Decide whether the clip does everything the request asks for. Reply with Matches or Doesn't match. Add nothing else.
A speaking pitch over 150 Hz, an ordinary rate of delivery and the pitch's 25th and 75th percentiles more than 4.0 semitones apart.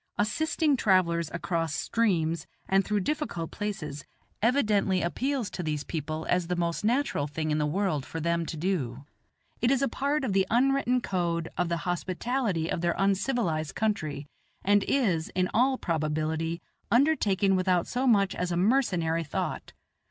Matches